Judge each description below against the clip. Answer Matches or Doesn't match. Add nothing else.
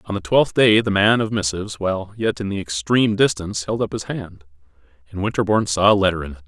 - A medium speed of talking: Doesn't match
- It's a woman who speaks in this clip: Doesn't match